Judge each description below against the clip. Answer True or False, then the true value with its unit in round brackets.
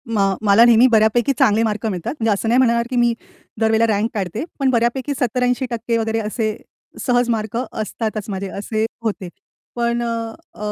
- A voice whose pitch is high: True (225 Hz)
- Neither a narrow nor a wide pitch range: False (1.8 semitones)